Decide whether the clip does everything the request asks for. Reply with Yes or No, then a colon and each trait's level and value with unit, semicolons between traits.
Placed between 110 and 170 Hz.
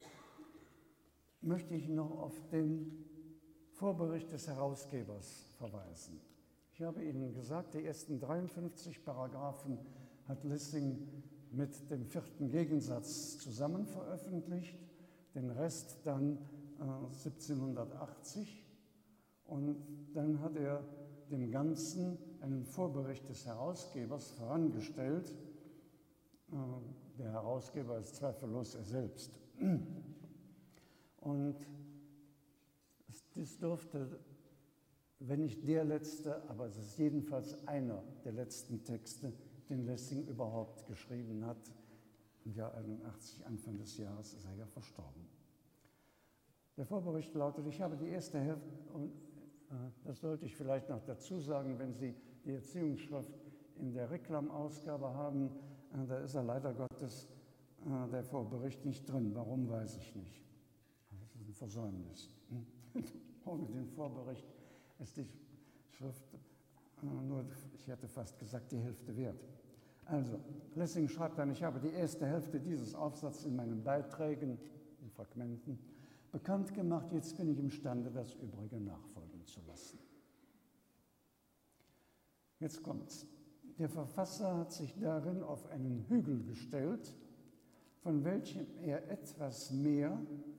Yes: medium, 140 Hz